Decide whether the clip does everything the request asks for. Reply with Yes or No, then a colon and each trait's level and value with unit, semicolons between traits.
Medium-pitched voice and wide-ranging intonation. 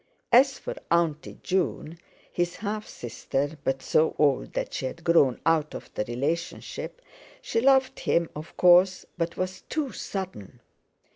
No: medium, 170 Hz; average, 4.4 semitones